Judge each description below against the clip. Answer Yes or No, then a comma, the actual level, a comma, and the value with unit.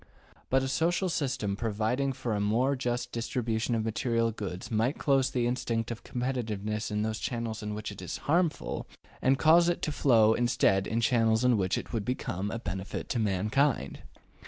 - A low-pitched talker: Yes, low, 115 Hz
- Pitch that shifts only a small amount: No, average, 3.4 semitones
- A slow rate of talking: No, average, 180 wpm